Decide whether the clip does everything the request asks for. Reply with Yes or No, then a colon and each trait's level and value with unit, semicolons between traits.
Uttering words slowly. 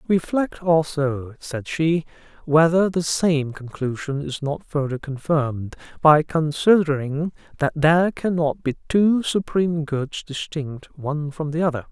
Yes: slow, 130 wpm